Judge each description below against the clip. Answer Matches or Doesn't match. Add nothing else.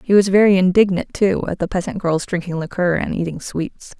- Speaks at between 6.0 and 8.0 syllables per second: Doesn't match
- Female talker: Matches